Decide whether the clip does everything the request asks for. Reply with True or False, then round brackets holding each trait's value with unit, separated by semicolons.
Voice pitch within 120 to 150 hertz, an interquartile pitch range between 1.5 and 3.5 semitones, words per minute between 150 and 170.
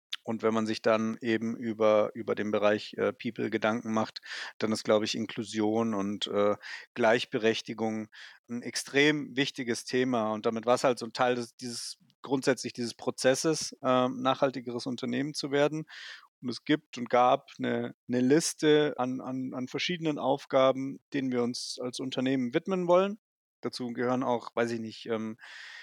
True (125 Hz; 3.1 semitones; 165 wpm)